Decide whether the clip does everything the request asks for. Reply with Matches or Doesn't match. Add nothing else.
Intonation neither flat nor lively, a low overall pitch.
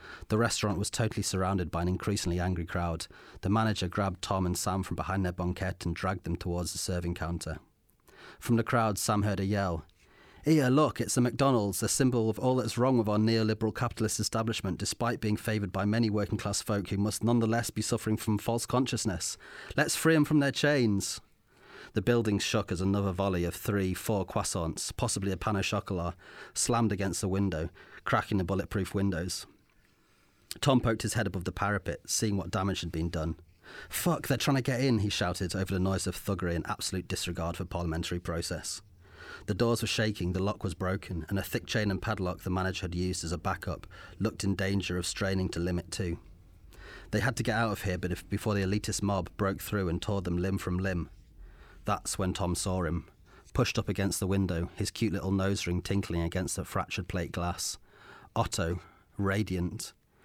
Matches